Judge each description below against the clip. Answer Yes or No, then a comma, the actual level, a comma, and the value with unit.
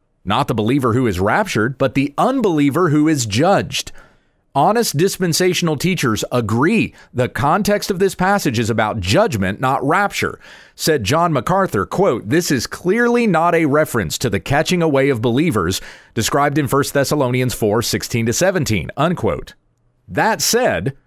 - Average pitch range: No, wide, 6.5 semitones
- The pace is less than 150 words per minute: Yes, average, 140 wpm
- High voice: No, medium, 140 Hz